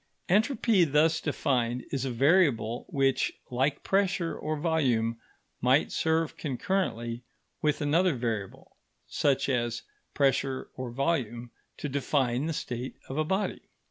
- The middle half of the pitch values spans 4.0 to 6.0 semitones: Yes, average, 4.8 semitones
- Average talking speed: No, slow, 125 wpm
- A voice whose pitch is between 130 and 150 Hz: Yes, medium, 140 Hz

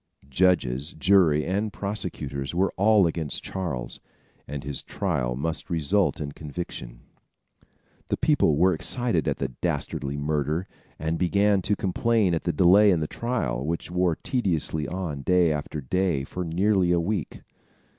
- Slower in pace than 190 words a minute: Yes, average, 145 wpm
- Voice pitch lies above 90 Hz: No, very low, 85 Hz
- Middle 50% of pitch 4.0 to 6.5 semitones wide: Yes, average, 4.5 semitones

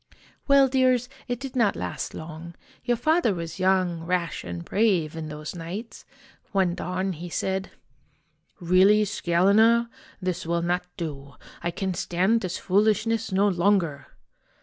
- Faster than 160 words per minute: No, average, 145 wpm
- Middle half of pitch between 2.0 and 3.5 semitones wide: No, average, 4.3 semitones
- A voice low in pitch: No, medium, 185 Hz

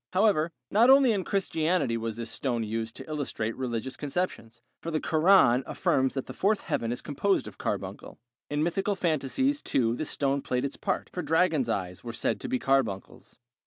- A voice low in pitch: No, medium, 145 Hz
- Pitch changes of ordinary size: No, wide, 7.4 semitones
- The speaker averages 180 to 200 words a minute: Yes, average, 185 wpm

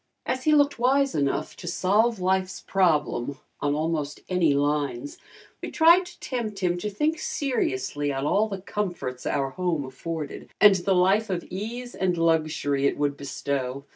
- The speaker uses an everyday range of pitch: No, wide, 6.6 semitones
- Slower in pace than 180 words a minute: Yes, average, 165 wpm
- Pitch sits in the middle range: Yes, medium, 175 Hz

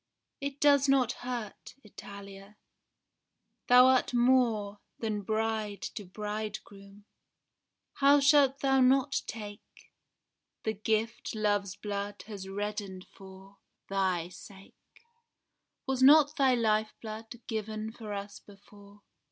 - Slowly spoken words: Yes, slow, 105 wpm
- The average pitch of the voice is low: No, high, 215 Hz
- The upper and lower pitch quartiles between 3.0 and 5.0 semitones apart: Yes, average, 3.8 semitones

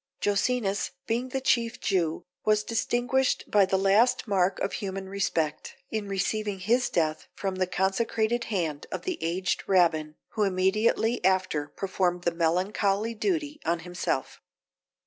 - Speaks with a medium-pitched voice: No, high, 195 Hz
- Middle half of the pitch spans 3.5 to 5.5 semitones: Yes, average, 3.9 semitones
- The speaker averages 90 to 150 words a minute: Yes, average, 140 wpm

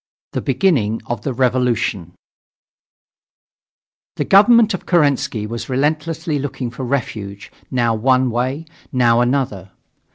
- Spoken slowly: Yes, slow, 110 wpm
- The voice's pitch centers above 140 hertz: No, low, 125 Hz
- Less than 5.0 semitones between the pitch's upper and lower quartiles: Yes, average, 4.0 semitones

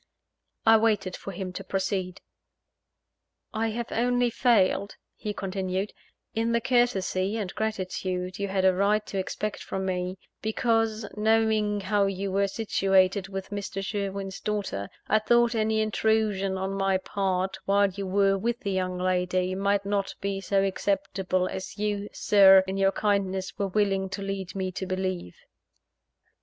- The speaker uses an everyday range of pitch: No, narrow, 2.0 semitones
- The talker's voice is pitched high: Yes, high, 195 Hz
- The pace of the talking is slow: No, average, 150 wpm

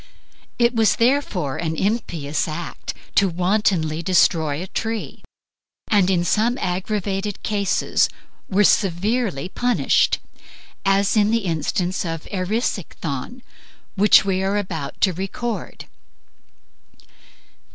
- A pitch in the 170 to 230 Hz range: Yes, high, 190 Hz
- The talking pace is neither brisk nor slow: No, slow, 105 wpm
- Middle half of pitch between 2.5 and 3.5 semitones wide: No, average, 3.9 semitones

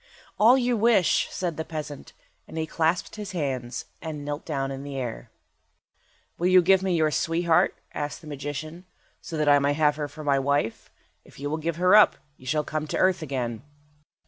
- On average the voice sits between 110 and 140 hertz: No, medium, 155 Hz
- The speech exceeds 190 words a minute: Yes, average, 200 wpm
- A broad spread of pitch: No, average, 3.5 semitones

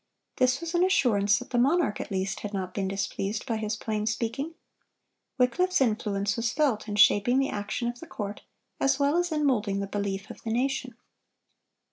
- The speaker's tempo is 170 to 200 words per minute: Yes, average, 190 wpm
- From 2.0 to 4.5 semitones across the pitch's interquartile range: No, average, 4.9 semitones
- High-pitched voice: Yes, high, 225 Hz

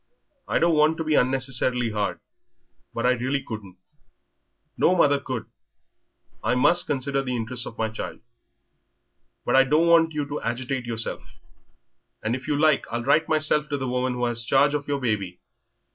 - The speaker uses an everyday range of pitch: Yes, average, 3.7 semitones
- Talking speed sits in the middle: Yes, average, 175 wpm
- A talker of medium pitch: No, low, 130 Hz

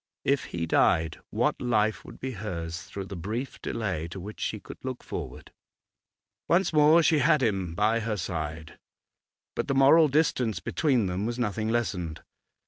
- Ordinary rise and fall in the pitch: No, wide, 6.5 semitones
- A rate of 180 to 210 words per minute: No, average, 165 wpm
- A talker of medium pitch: No, low, 110 Hz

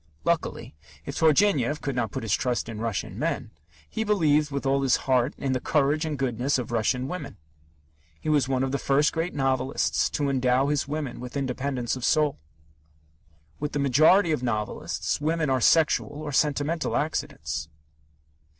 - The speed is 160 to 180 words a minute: Yes, average, 170 wpm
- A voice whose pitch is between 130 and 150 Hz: Yes, medium, 140 Hz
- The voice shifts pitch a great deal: No, average, 3.0 semitones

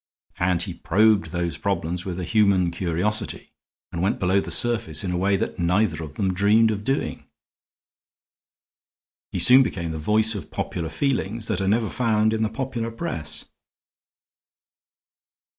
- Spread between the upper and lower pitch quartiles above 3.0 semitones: Yes, average, 4.1 semitones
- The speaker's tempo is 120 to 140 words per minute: No, average, 155 wpm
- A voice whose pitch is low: Yes, low, 100 Hz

